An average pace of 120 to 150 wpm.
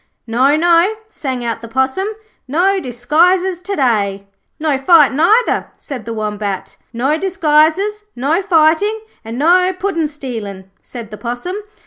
Yes: slow, 135 wpm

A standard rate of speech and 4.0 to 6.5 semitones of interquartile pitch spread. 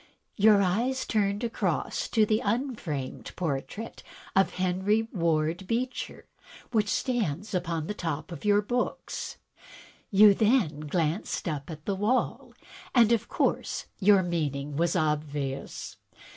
No: slow, 130 wpm; wide, 5.4 semitones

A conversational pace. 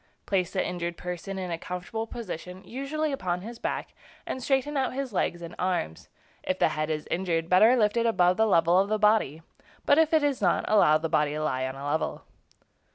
No: fast, 215 wpm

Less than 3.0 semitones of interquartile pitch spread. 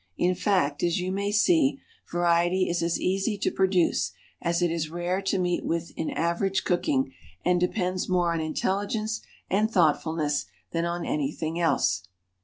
Yes: narrow, 2.4 semitones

